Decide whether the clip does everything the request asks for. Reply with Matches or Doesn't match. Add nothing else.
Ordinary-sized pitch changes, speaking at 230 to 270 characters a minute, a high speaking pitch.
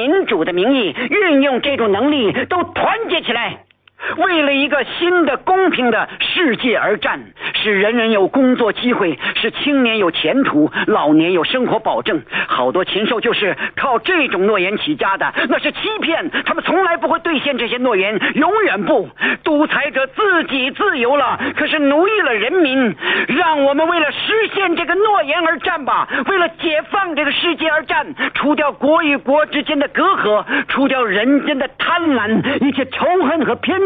Matches